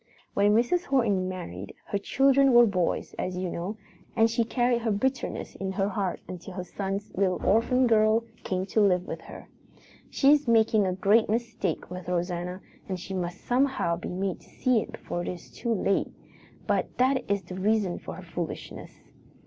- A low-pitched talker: No, high, 200 Hz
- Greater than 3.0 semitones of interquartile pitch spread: Yes, average, 4.2 semitones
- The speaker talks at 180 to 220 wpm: Yes, average, 185 wpm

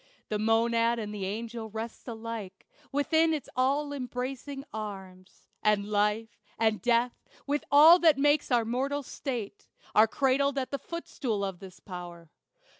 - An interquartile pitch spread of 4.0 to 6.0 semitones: Yes, average, 4.7 semitones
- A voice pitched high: Yes, high, 230 Hz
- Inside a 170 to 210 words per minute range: No, average, 145 wpm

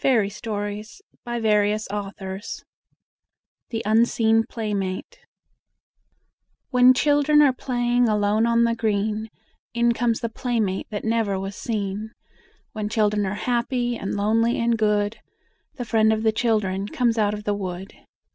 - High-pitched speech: Yes, high, 220 Hz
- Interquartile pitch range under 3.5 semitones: Yes, narrow, 2.4 semitones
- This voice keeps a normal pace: No, slow, 130 wpm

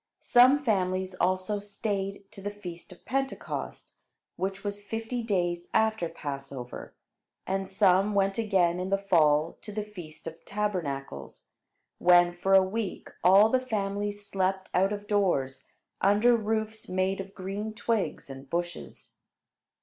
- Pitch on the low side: No, high, 195 Hz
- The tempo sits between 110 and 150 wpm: Yes, average, 140 wpm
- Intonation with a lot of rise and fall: No, average, 2.9 semitones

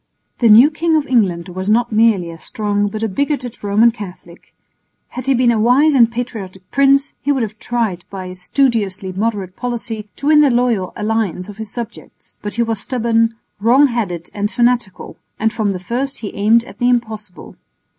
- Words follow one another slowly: No, average, 190 wpm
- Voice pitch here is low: No, high, 225 Hz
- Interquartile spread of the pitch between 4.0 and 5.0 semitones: No, average, 3.4 semitones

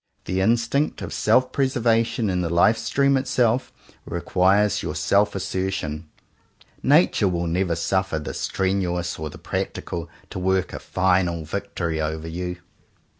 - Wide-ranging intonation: No, average, 3.6 semitones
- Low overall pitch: Yes, very low, 95 Hz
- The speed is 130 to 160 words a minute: Yes, average, 140 wpm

